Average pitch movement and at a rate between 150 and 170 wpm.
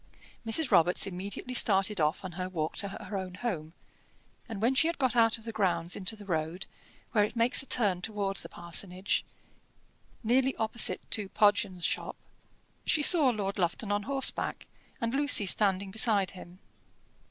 Yes: average, 3.9 semitones; average, 165 wpm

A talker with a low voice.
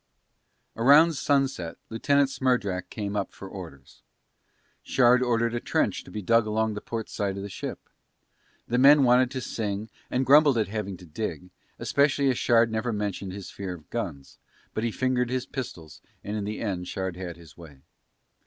Yes: low, 110 Hz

